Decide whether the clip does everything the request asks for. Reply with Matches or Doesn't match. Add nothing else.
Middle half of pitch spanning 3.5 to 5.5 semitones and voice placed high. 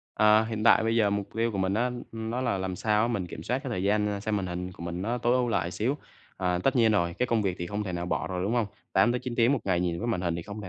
Doesn't match